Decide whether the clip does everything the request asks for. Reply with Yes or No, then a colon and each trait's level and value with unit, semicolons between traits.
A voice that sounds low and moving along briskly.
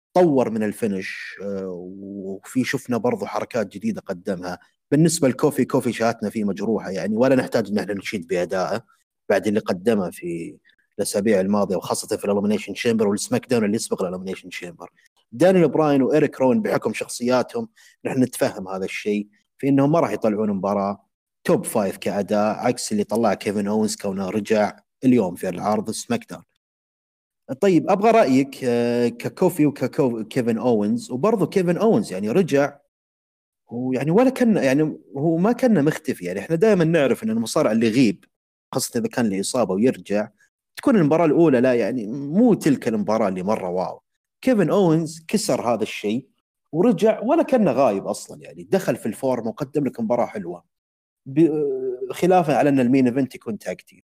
Yes: low, 130 Hz; fast, 155 wpm